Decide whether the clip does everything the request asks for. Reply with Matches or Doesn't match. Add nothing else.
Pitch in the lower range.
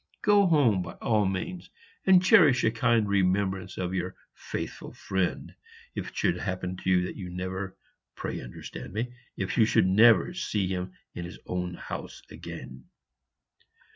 Matches